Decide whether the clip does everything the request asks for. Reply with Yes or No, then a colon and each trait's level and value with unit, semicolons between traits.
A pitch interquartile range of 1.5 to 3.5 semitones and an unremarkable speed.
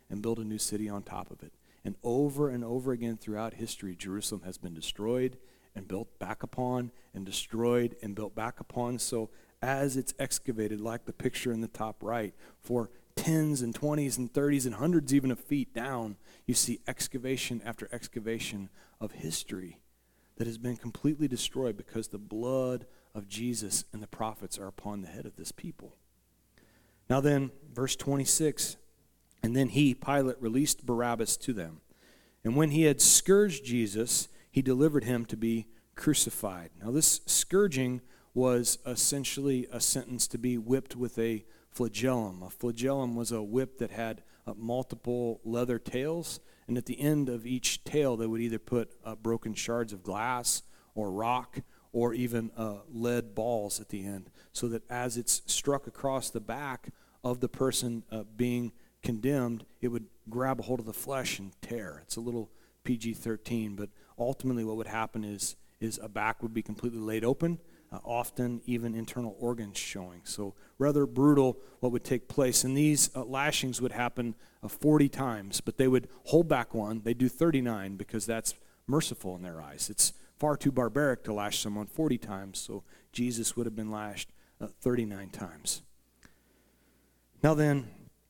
Yes: average, 2.9 semitones; average, 175 wpm